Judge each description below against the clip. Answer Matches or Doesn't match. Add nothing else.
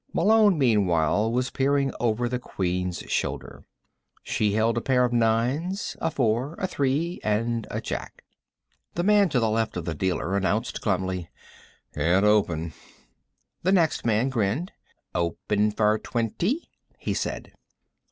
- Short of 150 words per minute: Matches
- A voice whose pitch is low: Matches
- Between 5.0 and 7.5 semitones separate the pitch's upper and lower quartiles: Matches